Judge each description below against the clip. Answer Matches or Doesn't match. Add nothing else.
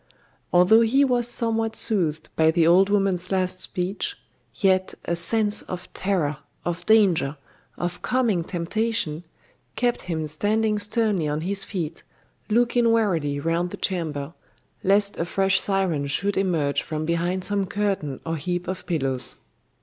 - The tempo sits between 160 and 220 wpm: Doesn't match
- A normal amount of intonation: Matches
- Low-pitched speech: Doesn't match